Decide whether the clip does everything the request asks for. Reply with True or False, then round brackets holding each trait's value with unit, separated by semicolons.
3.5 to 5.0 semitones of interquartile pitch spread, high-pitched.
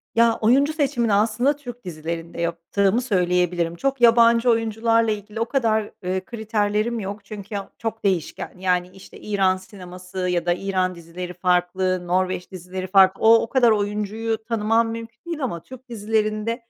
True (3.9 semitones; 210 Hz)